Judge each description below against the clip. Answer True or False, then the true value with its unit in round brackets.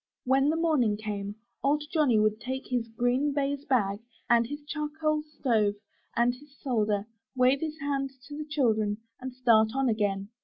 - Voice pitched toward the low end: False (255 Hz)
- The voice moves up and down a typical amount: True (5.0 semitones)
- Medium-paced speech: True (165 wpm)